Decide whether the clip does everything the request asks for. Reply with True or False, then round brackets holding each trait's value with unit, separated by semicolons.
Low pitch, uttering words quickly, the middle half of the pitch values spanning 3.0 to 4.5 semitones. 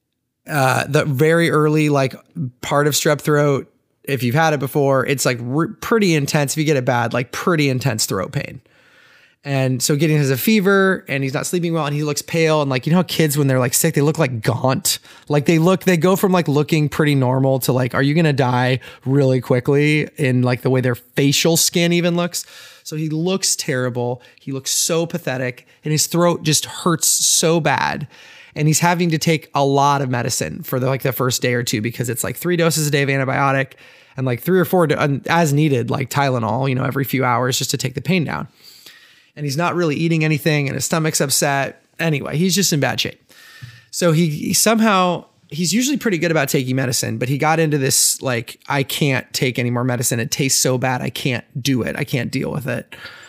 False (145 Hz; 225 wpm; 3.9 semitones)